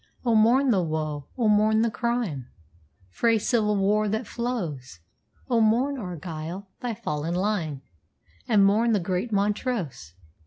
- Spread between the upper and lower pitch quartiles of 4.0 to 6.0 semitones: Yes, wide, 5.5 semitones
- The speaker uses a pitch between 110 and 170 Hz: No, high, 210 Hz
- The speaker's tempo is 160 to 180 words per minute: No, average, 140 wpm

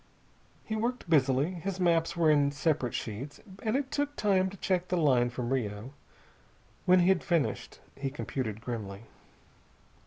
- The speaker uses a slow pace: No, average, 155 wpm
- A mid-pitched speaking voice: Yes, medium, 155 Hz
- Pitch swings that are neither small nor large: No, wide, 6.4 semitones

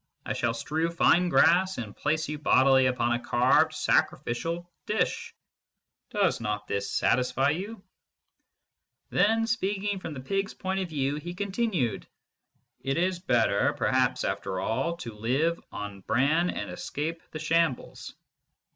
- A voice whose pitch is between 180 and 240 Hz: No, medium, 160 Hz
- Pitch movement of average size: No, wide, 6.9 semitones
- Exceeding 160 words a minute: No, average, 140 wpm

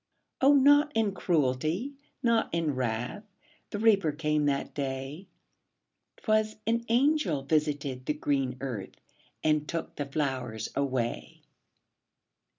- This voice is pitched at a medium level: Yes, medium, 150 Hz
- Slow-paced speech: Yes, slow, 115 wpm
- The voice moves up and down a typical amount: No, wide, 8.1 semitones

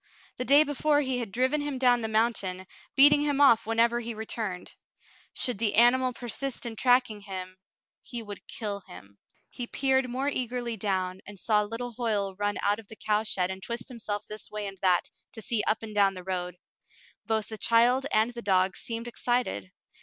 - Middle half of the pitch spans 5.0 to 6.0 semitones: No, average, 3.5 semitones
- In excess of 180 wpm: Yes, average, 190 wpm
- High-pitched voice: Yes, high, 225 Hz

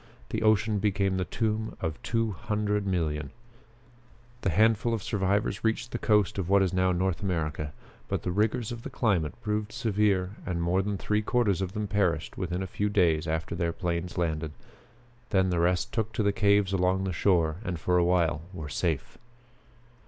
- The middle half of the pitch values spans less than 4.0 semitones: Yes, average, 3.3 semitones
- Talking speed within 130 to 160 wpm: No, average, 185 wpm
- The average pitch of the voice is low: Yes, very low, 95 Hz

